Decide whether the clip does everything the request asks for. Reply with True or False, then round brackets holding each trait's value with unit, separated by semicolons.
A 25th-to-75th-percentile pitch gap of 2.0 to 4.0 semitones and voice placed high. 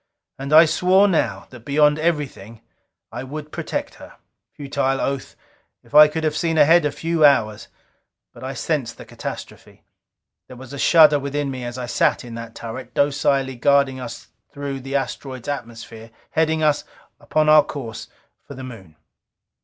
False (3.2 semitones; 140 Hz)